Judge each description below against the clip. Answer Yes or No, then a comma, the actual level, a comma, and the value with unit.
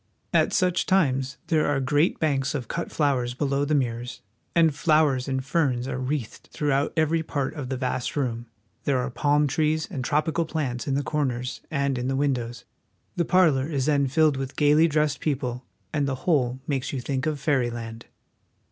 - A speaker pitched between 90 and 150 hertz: Yes, medium, 140 Hz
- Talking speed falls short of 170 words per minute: No, average, 185 wpm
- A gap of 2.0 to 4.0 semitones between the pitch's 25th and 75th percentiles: Yes, average, 2.9 semitones